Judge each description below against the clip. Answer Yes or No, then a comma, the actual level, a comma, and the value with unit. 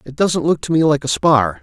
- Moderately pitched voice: Yes, medium, 145 Hz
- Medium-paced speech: No, fast, 295 wpm